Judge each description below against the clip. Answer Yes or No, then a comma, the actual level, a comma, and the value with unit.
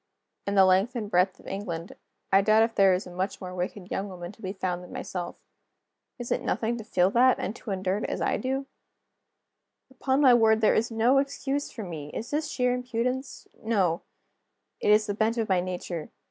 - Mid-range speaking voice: No, high, 210 Hz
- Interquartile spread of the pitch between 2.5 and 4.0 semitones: No, average, 4.4 semitones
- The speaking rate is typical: No, fast, 210 wpm